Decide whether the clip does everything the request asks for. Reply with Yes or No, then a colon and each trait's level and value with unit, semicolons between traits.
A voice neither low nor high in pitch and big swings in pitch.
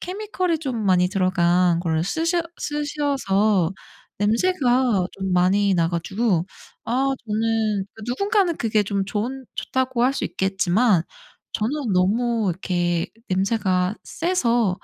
No: high, 215 Hz; wide, 5.9 semitones